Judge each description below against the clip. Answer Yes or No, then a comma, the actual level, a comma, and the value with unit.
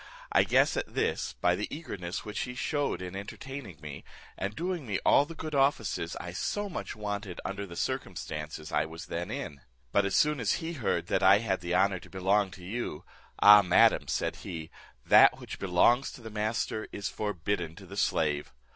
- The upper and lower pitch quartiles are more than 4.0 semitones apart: Yes, wide, 5.5 semitones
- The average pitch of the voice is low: Yes, low, 100 Hz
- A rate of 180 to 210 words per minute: Yes, average, 195 wpm